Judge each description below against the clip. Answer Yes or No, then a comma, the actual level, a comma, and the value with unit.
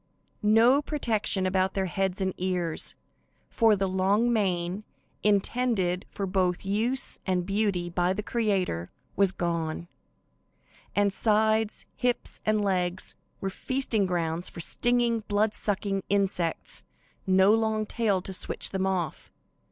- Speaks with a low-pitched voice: No, high, 195 Hz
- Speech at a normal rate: No, slow, 130 wpm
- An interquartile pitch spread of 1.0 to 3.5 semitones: Yes, average, 2.9 semitones